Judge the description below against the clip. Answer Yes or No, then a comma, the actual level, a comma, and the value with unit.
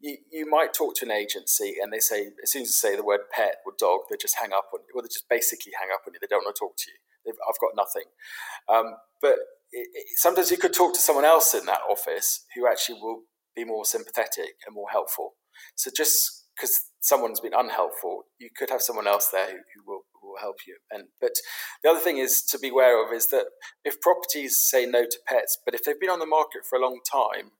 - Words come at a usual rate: No, fast, 250 wpm